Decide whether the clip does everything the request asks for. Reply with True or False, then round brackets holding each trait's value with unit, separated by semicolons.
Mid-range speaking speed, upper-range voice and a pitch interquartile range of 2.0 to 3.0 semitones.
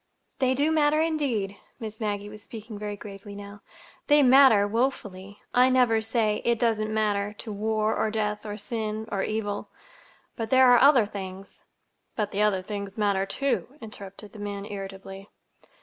True (160 wpm; 215 Hz; 2.6 semitones)